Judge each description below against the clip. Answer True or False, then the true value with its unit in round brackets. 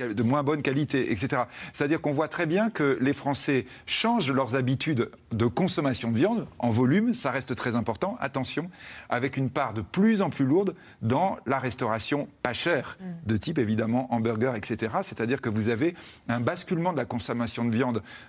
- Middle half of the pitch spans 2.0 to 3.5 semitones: False (3.9 semitones)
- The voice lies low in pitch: True (130 Hz)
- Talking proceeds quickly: False (185 wpm)